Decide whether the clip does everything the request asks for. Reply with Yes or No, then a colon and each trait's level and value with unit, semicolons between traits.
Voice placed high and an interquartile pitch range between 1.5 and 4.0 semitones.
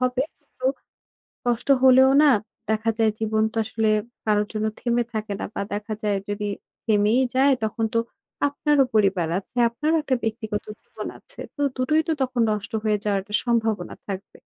Yes: high, 220 Hz; average, 3.5 semitones